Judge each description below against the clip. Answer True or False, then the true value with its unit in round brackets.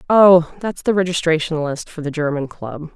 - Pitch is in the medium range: True (165 Hz)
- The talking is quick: False (185 wpm)